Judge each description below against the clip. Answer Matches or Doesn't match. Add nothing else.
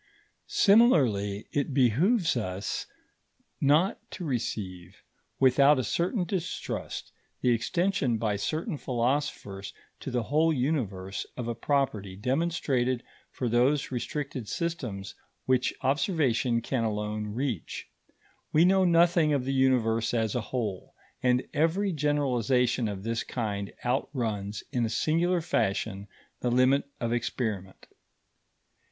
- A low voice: Matches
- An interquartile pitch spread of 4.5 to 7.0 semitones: Matches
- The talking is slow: Matches